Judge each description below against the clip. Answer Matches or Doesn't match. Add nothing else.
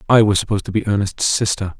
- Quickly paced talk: Matches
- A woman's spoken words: Doesn't match